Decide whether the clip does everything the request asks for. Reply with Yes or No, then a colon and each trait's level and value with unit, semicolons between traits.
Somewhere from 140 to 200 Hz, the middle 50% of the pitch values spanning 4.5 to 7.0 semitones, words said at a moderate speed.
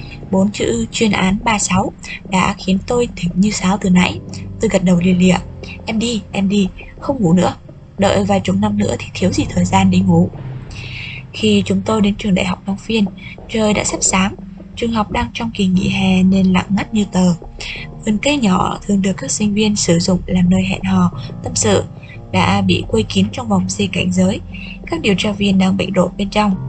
No: high, 190 Hz; average, 3.3 semitones; average, 215 wpm